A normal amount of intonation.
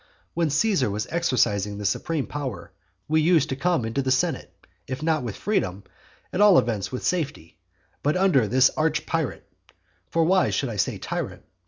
No: wide, 6.7 semitones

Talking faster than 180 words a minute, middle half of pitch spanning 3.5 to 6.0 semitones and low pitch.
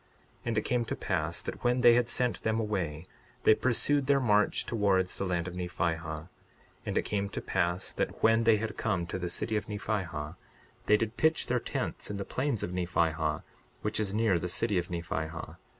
Yes: fast, 205 wpm; average, 4.6 semitones; low, 100 Hz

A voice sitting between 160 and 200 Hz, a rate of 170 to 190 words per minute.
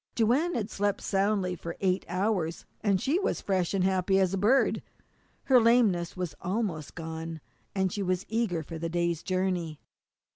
Yes: high, 190 Hz; average, 180 wpm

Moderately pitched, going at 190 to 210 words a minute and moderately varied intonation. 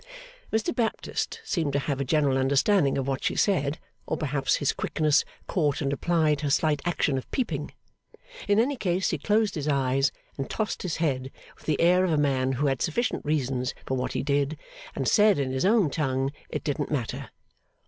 Yes: medium, 145 Hz; average, 195 wpm; average, 4.2 semitones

